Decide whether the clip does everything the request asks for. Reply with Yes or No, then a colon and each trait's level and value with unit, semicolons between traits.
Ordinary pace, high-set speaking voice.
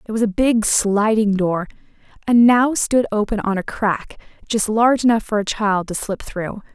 Yes: average, 195 wpm; high, 215 Hz